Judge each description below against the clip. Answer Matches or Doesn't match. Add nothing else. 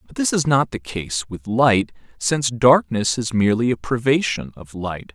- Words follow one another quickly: Doesn't match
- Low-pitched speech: Matches